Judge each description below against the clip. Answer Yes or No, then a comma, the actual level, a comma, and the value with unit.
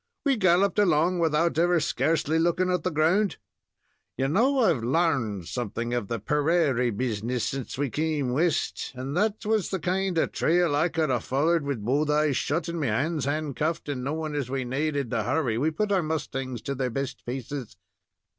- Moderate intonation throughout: Yes, average, 4.6 semitones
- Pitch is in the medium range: Yes, medium, 150 Hz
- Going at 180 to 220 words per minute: Yes, average, 185 wpm